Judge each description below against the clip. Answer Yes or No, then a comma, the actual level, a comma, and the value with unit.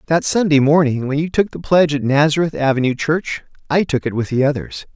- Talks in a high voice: No, medium, 145 Hz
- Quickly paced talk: Yes, fast, 220 wpm